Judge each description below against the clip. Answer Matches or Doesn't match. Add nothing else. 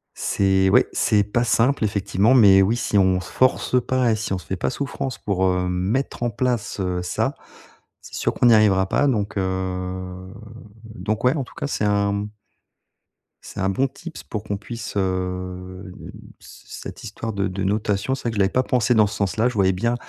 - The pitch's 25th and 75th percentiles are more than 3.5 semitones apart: Matches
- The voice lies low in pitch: Matches